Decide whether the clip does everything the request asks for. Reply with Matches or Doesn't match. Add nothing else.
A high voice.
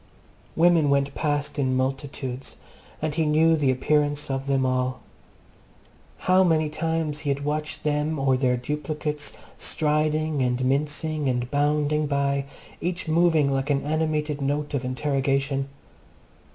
Doesn't match